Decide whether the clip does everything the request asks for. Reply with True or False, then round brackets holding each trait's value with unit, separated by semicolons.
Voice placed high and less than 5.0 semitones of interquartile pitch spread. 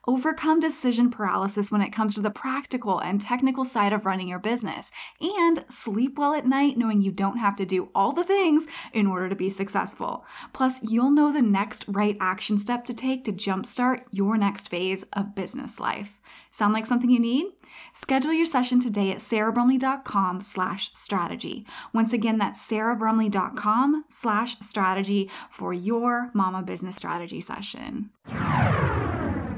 True (220 Hz; 4.6 semitones)